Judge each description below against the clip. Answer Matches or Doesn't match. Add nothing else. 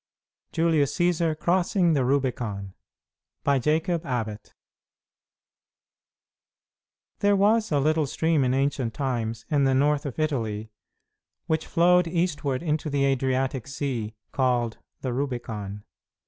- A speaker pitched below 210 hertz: Matches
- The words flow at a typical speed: Doesn't match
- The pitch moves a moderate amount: Matches